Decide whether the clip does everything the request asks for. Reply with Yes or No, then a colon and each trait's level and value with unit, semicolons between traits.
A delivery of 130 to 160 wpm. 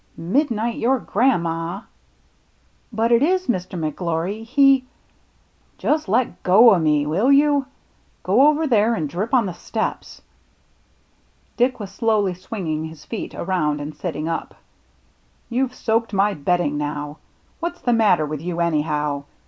Yes: average, 155 wpm